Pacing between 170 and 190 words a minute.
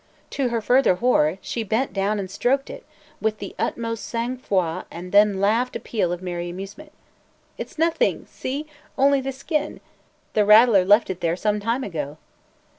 Yes: average, 180 wpm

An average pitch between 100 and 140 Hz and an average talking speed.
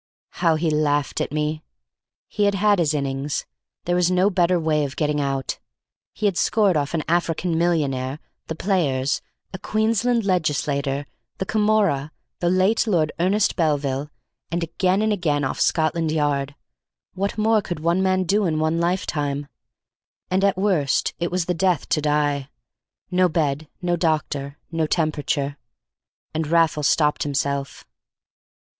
No: medium, 160 Hz; average, 150 wpm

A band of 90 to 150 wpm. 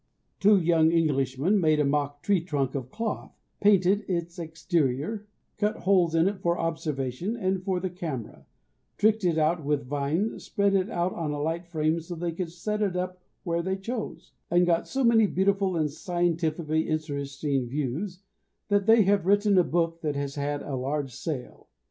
No: average, 180 wpm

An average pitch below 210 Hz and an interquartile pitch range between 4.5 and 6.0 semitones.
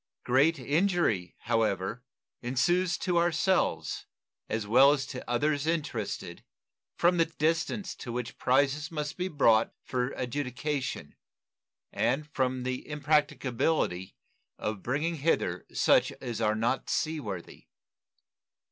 Yes: low, 135 Hz; average, 4.9 semitones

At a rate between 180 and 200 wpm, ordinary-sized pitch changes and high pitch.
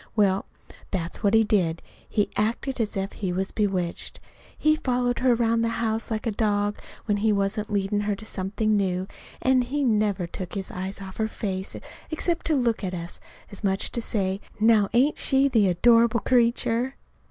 Yes: average, 185 wpm; average, 3.3 semitones; high, 215 Hz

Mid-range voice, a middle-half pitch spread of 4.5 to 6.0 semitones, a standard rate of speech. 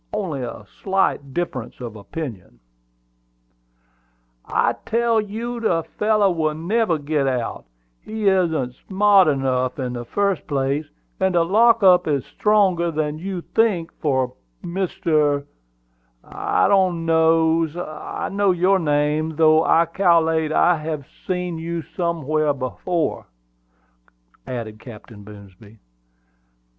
No: medium, 160 Hz; average, 5.0 semitones; slow, 120 wpm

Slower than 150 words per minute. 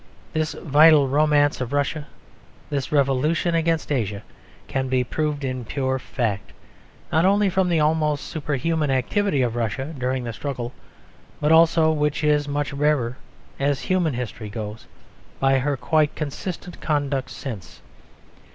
Yes: average, 140 wpm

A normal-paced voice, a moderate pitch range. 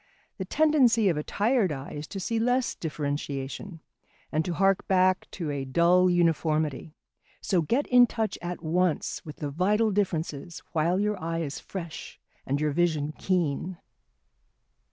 Yes: average, 155 wpm; average, 4.3 semitones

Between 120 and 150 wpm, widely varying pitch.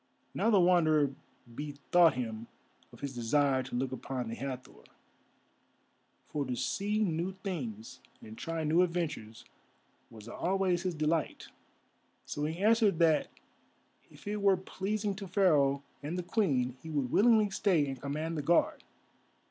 Yes: average, 145 wpm; wide, 5.8 semitones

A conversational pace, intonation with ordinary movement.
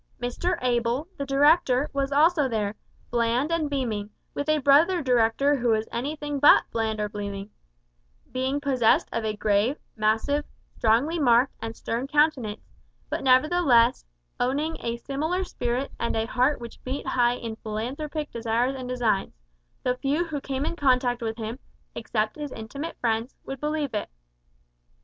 Yes: average, 155 wpm; average, 4.1 semitones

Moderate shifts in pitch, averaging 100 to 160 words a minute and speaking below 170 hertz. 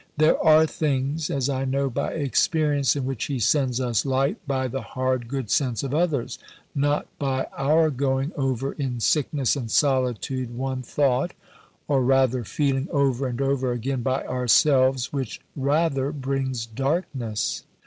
No: narrow, 1.7 semitones; average, 150 wpm; low, 135 Hz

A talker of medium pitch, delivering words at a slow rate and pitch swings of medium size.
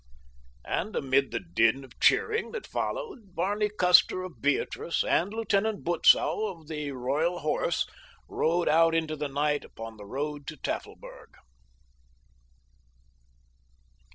No: medium, 160 Hz; slow, 125 wpm; wide, 5.7 semitones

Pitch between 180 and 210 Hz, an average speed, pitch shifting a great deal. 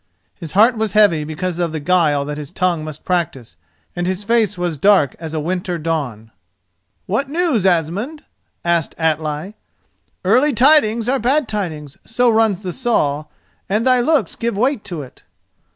Yes: medium, 185 Hz; average, 165 wpm; wide, 6.4 semitones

